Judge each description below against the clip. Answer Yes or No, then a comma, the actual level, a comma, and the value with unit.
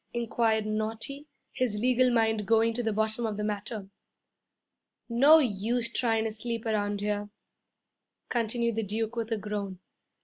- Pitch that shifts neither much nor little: No, narrow, 2.0 semitones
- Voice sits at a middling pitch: No, high, 225 Hz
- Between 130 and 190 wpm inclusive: Yes, average, 145 wpm